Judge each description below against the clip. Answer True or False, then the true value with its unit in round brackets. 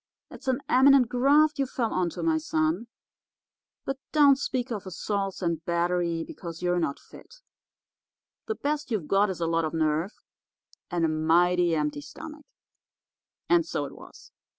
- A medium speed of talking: True (155 wpm)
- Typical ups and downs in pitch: False (8.6 semitones)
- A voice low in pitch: False (195 Hz)